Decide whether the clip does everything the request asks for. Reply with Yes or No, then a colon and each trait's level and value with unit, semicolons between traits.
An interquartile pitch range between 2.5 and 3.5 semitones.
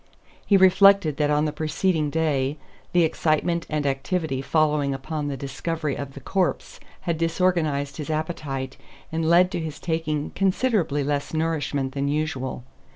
Yes: average, 2.8 semitones